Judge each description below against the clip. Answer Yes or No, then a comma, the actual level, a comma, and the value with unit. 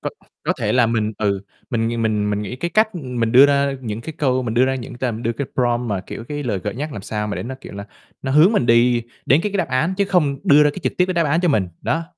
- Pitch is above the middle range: No, low, 125 Hz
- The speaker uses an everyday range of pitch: Yes, average, 4.6 semitones